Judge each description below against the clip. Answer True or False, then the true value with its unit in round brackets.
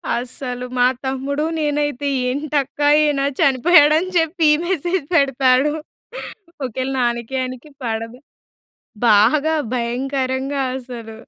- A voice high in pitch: True (270 Hz)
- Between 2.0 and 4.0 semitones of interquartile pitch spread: True (3.0 semitones)